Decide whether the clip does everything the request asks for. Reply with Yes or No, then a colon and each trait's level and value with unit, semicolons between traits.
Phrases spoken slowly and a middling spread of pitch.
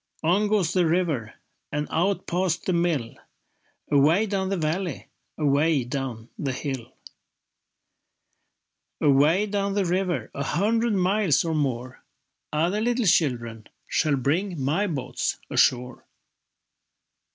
No: slow, 120 wpm; wide, 5.7 semitones